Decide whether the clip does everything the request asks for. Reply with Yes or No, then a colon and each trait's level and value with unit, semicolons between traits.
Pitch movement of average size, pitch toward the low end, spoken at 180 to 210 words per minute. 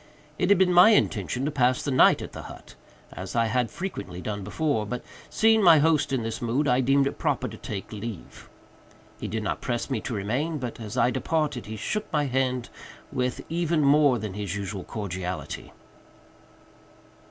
No: wide, 5.7 semitones; low, 125 Hz; average, 185 wpm